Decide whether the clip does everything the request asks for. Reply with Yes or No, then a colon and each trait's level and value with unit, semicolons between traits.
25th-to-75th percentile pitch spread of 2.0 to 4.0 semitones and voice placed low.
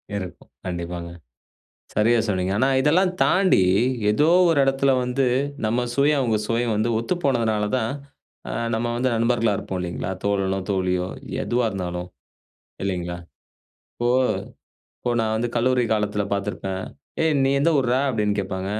No: average, 4.8 semitones; low, 110 Hz